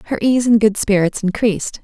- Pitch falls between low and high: No, high, 215 Hz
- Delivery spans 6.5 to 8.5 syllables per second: No, 5.7 syllables/s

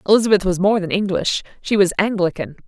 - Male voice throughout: No, female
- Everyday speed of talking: Yes, average, 155 wpm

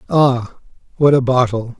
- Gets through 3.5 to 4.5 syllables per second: Yes, 4.0 syllables/s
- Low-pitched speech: Yes, low, 125 Hz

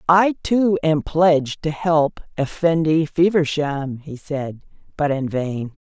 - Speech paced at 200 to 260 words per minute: No, slow, 135 wpm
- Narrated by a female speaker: Yes, female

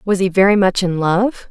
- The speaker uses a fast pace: Yes, fast, 240 wpm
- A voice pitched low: No, high, 190 Hz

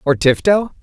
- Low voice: No, medium, 170 Hz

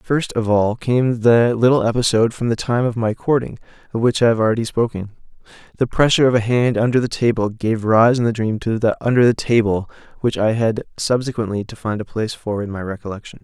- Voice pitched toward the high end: No, low, 115 Hz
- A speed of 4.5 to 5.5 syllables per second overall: No, 5.9 syllables/s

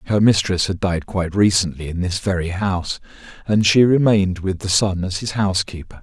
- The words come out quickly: No, average, 190 wpm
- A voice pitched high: No, very low, 95 Hz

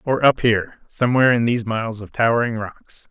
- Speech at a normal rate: Yes, average, 195 wpm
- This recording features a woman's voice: No, male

